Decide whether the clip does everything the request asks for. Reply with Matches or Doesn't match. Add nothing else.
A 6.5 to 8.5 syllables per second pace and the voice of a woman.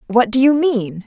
Doesn't match